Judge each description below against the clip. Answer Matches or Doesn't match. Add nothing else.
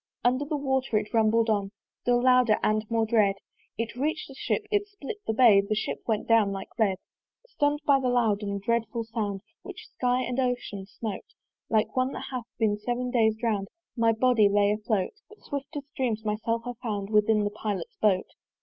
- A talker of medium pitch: Doesn't match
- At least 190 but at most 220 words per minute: Matches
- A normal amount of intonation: Matches